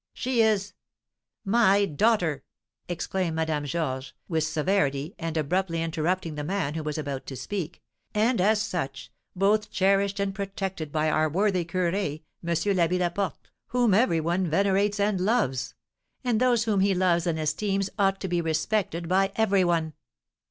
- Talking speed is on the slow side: No, average, 160 wpm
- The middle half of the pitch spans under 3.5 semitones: No, average, 3.9 semitones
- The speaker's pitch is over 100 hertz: Yes, medium, 185 Hz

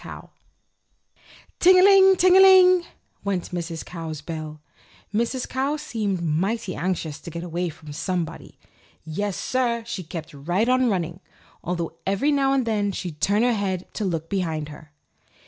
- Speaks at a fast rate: No, average, 160 wpm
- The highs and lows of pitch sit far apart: Yes, wide, 7.0 semitones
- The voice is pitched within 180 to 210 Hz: Yes, high, 190 Hz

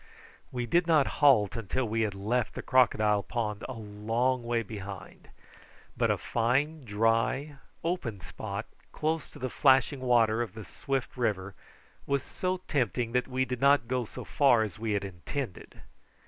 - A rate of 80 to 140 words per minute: No, average, 160 wpm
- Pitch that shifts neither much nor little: Yes, average, 3.7 semitones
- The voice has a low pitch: Yes, low, 120 Hz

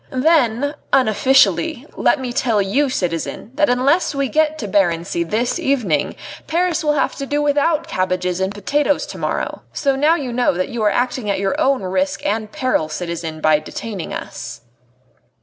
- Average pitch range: No, wide, 7.1 semitones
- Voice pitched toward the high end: Yes, high, 245 Hz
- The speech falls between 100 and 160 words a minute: No, average, 170 wpm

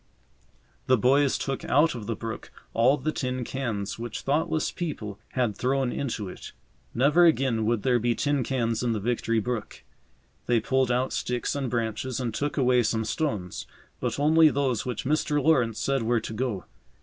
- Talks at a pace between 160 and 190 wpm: Yes, average, 175 wpm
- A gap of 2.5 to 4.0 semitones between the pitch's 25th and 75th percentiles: Yes, average, 3.2 semitones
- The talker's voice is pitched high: No, low, 125 Hz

